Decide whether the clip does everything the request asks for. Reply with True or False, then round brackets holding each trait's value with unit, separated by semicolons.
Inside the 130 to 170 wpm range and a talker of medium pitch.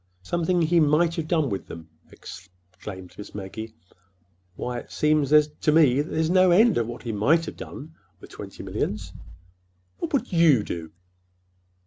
True (150 wpm; 145 Hz)